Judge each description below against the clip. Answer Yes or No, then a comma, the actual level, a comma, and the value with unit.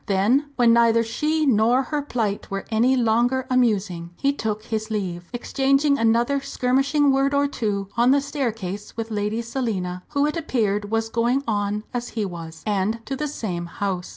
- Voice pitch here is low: No, high, 230 Hz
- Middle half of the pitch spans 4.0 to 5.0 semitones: Yes, average, 4.5 semitones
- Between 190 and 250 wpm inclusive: No, average, 175 wpm